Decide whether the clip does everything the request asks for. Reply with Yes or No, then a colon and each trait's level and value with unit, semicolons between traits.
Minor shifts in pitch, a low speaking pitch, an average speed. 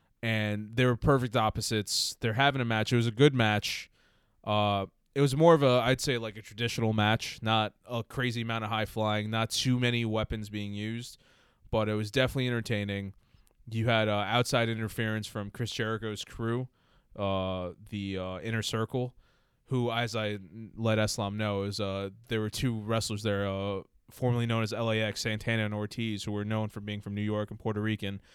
Yes: narrow, 2.0 semitones; low, 110 Hz; average, 190 wpm